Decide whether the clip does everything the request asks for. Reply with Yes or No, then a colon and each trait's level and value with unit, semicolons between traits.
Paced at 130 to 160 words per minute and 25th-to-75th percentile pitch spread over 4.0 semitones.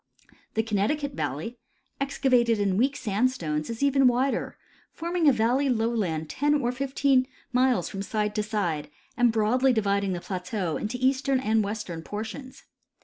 Yes: average, 150 wpm; average, 4.7 semitones